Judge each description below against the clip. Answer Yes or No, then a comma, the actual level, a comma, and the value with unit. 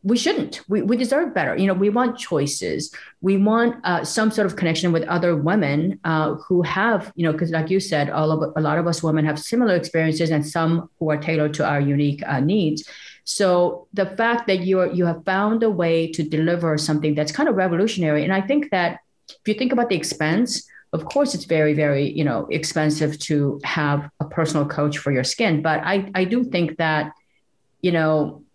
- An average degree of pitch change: Yes, average, 4.2 semitones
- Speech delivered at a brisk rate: Yes, fast, 210 wpm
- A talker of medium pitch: Yes, medium, 165 Hz